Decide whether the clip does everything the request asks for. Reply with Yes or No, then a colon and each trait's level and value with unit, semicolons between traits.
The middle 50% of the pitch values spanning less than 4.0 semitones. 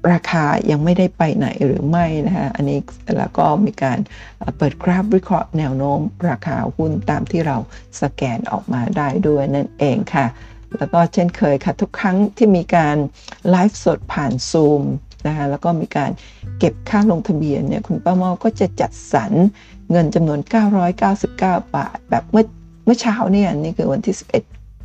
No: average, 5.1 semitones